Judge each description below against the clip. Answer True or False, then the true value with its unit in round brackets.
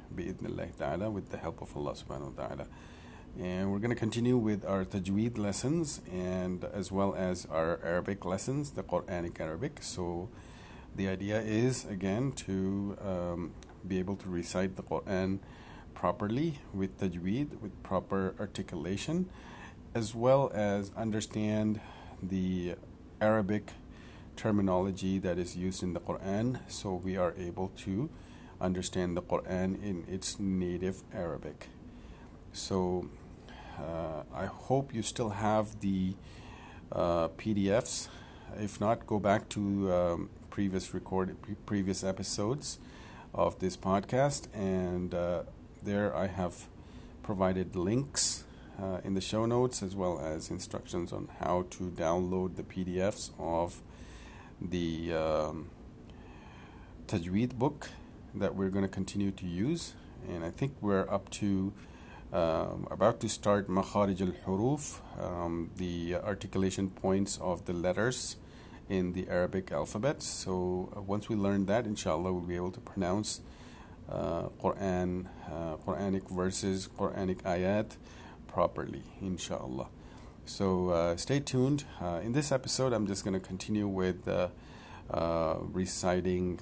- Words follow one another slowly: True (130 wpm)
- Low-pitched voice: True (95 Hz)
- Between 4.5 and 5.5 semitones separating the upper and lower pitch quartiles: False (2.8 semitones)